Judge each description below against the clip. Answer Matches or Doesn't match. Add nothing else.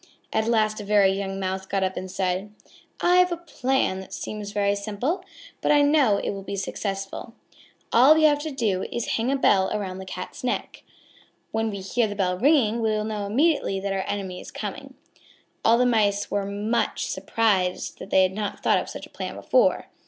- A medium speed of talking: Doesn't match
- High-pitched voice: Matches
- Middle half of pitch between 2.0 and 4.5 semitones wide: Matches